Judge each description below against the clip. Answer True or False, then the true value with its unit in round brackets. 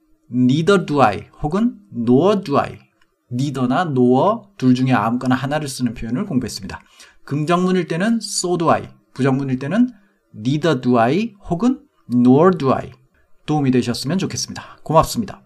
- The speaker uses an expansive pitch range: True (6.7 semitones)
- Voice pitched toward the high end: False (135 Hz)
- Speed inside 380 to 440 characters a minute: True (395 characters per minute)